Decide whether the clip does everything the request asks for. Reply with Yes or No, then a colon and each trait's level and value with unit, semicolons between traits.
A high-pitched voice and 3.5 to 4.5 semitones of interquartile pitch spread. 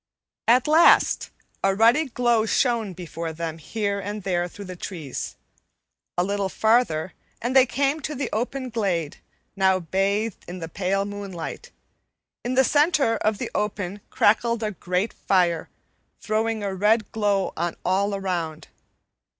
Yes: high, 205 Hz; average, 4.1 semitones